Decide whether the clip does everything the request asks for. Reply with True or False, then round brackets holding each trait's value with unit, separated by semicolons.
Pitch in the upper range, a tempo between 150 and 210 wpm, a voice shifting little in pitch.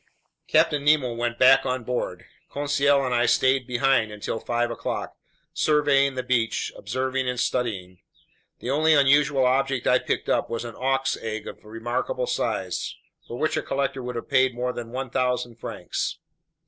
False (130 Hz; 160 wpm; 2.3 semitones)